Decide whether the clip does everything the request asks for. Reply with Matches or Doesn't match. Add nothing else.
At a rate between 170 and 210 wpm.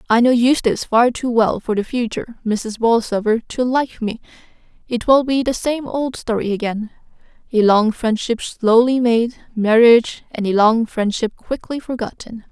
Doesn't match